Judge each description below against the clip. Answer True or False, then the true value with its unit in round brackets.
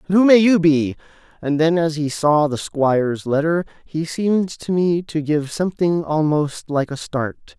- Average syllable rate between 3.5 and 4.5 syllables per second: True (4.4 syllables/s)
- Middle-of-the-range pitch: True (160 Hz)